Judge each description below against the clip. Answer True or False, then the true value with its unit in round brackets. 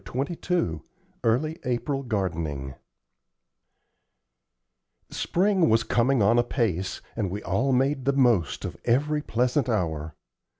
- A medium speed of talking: False (115 wpm)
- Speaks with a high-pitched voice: False (120 Hz)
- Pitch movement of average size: False (6.2 semitones)